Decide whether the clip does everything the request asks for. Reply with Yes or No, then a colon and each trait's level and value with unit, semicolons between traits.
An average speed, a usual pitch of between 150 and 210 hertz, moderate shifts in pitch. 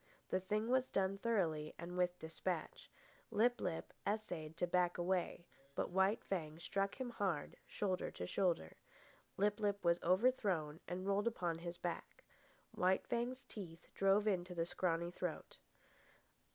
Yes: average, 145 wpm; medium, 185 Hz; average, 3.1 semitones